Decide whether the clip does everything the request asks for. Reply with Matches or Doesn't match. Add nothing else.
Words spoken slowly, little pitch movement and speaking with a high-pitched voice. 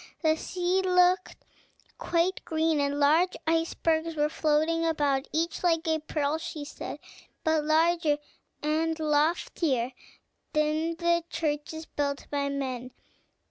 Matches